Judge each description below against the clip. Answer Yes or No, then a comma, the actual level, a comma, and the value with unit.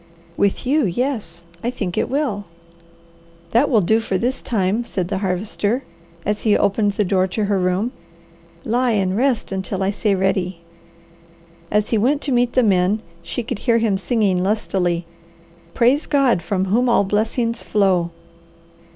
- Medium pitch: No, high, 210 Hz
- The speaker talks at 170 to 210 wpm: No, average, 160 wpm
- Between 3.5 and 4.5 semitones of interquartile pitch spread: Yes, average, 3.9 semitones